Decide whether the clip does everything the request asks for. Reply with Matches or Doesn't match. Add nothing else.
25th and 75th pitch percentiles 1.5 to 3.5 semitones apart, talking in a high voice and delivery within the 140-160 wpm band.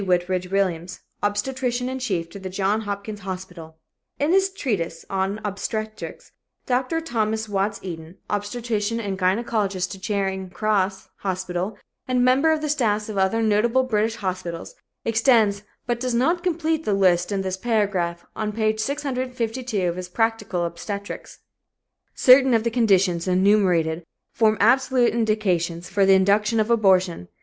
Doesn't match